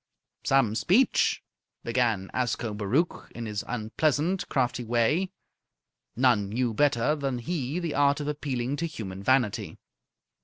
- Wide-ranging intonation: No, average, 4.5 semitones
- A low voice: Yes, low, 125 Hz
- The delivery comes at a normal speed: No, slow, 120 wpm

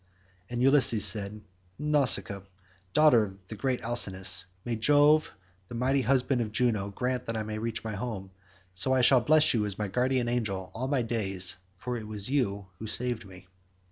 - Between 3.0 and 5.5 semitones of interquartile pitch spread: Yes, average, 3.7 semitones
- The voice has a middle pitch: No, low, 115 Hz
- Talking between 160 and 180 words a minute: Yes, average, 175 wpm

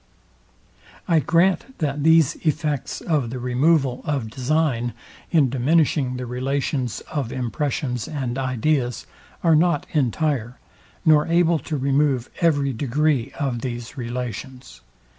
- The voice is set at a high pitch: No, low, 135 Hz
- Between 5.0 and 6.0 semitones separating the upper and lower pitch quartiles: No, average, 3.7 semitones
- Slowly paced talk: Yes, slow, 120 wpm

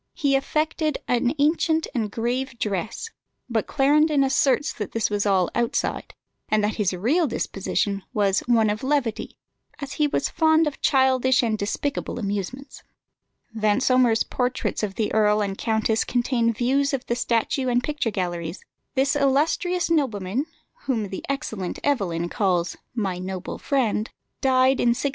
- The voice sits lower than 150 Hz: No, high, 240 Hz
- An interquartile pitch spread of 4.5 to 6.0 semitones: Yes, average, 4.9 semitones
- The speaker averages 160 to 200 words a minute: No, average, 150 wpm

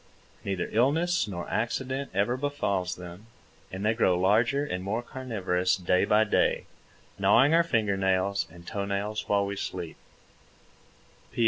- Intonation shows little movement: No, average, 4.6 semitones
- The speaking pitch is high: No, low, 100 Hz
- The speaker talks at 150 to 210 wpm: No, average, 140 wpm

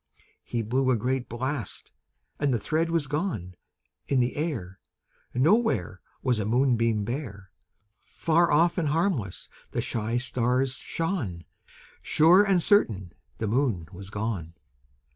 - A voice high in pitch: No, low, 125 Hz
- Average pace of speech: No, slow, 130 wpm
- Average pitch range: No, wide, 6.4 semitones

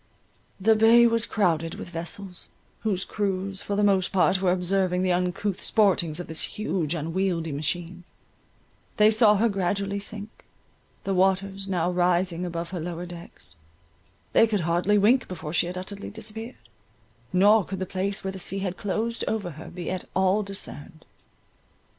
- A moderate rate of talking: Yes, average, 155 wpm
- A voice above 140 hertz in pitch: Yes, medium, 185 Hz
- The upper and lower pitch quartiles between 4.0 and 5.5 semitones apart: No, average, 2.7 semitones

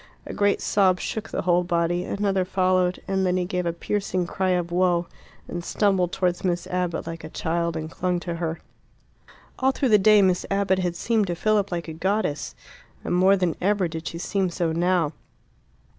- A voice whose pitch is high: No, medium, 180 Hz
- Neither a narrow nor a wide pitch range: No, narrow, 2.1 semitones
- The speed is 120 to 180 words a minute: No, average, 195 wpm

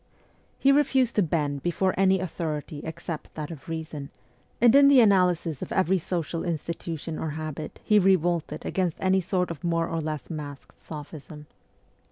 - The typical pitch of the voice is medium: Yes, medium, 165 Hz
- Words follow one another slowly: No, average, 160 wpm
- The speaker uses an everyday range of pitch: Yes, average, 3.4 semitones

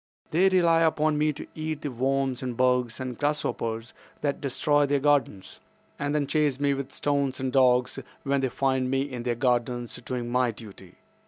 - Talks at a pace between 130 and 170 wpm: No, average, 180 wpm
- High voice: No, low, 135 Hz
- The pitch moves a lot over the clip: No, average, 2.7 semitones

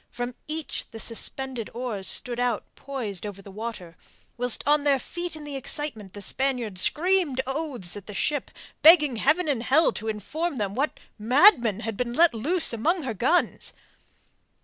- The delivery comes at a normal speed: Yes, average, 170 wpm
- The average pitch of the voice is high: Yes, very high, 250 Hz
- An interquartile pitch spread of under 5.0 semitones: No, wide, 5.4 semitones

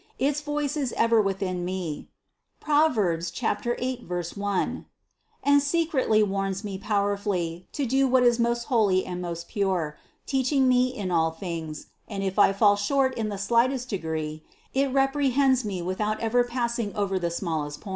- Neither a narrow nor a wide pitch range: No, wide, 5.7 semitones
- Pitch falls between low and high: No, high, 210 Hz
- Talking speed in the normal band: Yes, average, 165 wpm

